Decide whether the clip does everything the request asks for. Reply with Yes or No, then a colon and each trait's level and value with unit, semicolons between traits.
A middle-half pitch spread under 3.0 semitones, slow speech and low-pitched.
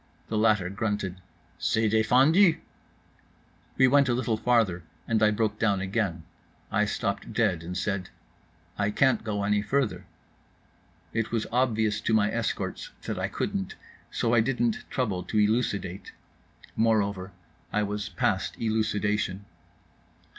Yes: narrow, 2.5 semitones; slow, 130 wpm; low, 105 Hz